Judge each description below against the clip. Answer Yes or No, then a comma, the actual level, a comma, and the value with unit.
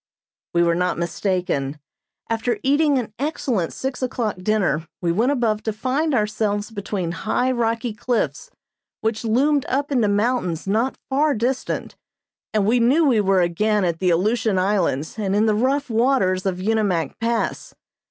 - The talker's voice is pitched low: No, high, 215 Hz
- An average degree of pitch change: Yes, average, 5.0 semitones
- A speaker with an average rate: Yes, average, 155 wpm